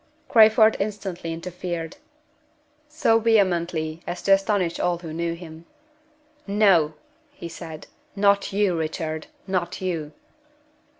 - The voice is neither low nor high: Yes, medium, 180 Hz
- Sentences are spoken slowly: Yes, slow, 110 wpm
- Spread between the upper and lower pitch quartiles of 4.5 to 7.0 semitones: No, average, 3.4 semitones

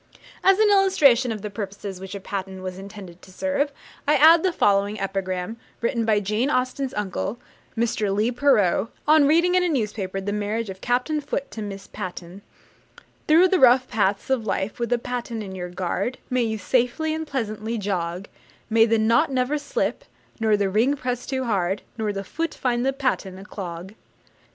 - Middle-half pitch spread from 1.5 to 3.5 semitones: No, average, 5.2 semitones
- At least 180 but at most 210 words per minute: Yes, average, 185 wpm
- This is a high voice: Yes, high, 225 Hz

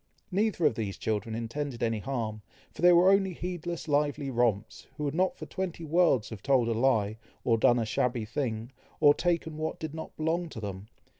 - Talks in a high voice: No, low, 135 Hz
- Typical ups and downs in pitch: No, wide, 6.5 semitones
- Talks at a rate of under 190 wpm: No, average, 200 wpm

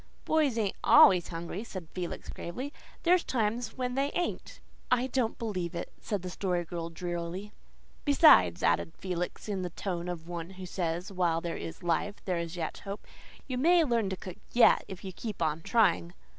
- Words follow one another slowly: No, average, 185 wpm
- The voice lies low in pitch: No, medium, 185 Hz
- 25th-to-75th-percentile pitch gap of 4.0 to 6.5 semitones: Yes, average, 5.2 semitones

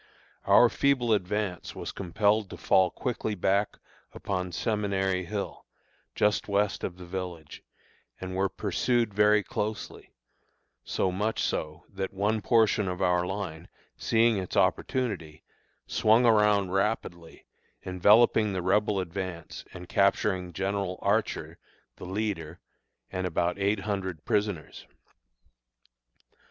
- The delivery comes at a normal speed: No, slow, 120 wpm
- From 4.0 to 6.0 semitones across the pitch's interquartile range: No, narrow, 2.5 semitones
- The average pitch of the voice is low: Yes, low, 100 Hz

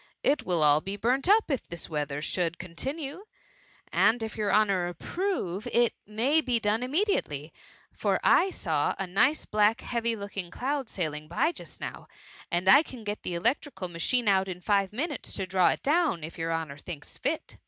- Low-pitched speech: No, high, 205 Hz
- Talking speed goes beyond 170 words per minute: Yes, average, 185 wpm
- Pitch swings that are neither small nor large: No, wide, 7.3 semitones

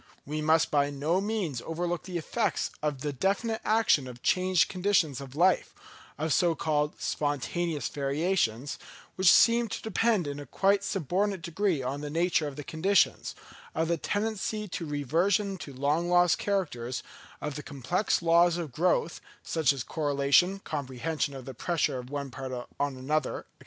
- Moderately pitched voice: Yes, medium, 160 Hz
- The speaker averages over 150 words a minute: Yes, average, 165 wpm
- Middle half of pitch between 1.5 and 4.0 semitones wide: No, average, 4.6 semitones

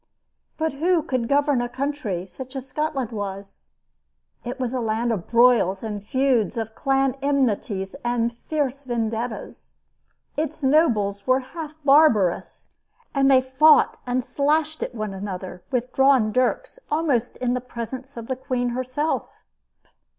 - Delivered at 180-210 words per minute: No, average, 145 wpm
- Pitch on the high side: Yes, very high, 255 Hz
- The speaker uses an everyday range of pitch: Yes, average, 3.8 semitones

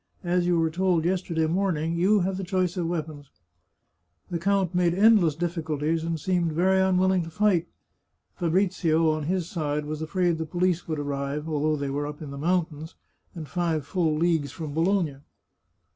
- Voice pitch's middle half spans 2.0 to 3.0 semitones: Yes, average, 2.7 semitones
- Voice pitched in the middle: Yes, medium, 165 Hz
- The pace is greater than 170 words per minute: Yes, average, 180 wpm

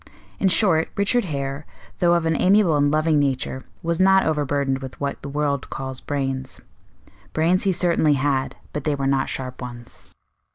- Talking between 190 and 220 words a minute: No, average, 175 wpm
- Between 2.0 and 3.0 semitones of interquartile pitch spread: No, average, 3.8 semitones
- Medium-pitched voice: Yes, medium, 145 Hz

